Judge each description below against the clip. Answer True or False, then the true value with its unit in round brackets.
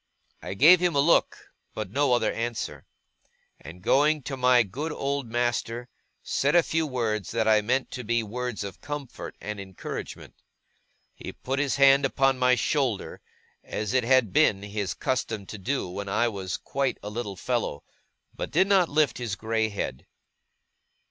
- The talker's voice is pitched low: True (120 Hz)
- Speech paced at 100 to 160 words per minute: False (170 wpm)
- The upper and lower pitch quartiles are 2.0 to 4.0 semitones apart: False (4.4 semitones)